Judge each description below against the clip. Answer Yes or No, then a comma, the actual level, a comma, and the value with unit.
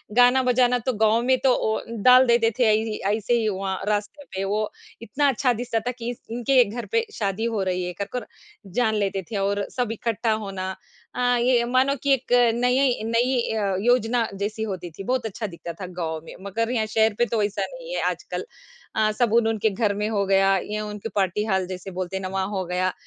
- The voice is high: Yes, high, 220 Hz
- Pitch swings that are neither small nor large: Yes, average, 3.7 semitones